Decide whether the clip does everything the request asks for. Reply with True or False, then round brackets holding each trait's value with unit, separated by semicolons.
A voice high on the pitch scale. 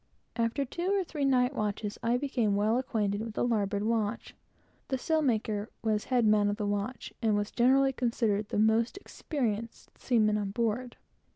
True (225 Hz)